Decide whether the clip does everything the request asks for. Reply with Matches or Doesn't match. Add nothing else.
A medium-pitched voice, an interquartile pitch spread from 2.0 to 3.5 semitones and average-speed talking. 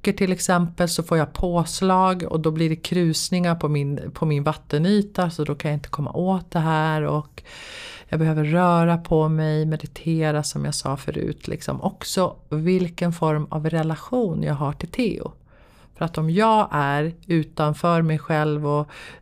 Matches